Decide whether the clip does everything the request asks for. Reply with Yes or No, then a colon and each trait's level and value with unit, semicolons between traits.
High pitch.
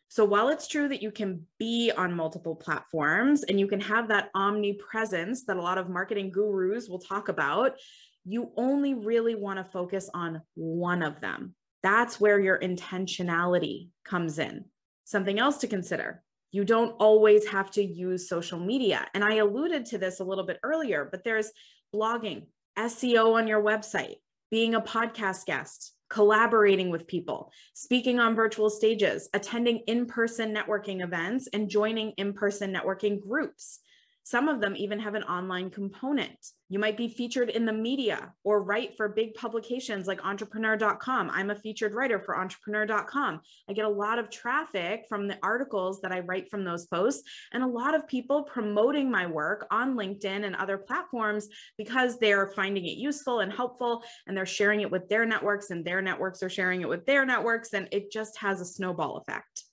Yes: high, 210 Hz